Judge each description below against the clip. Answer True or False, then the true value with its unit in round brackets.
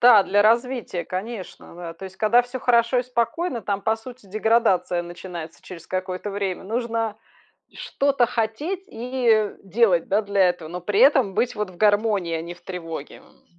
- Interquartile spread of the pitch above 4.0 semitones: True (4.4 semitones)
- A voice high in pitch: True (210 Hz)